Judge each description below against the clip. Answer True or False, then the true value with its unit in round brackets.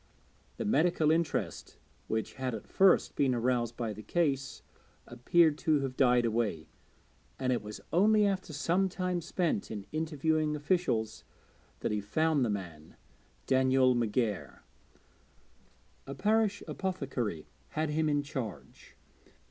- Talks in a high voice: False (140 Hz)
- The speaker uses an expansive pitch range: True (5.8 semitones)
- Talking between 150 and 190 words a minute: False (135 wpm)